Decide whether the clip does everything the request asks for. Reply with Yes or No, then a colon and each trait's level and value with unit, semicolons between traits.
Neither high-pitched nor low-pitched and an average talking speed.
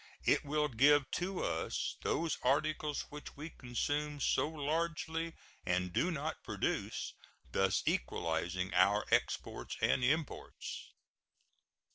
No: medium, 145 Hz; slow, 110 wpm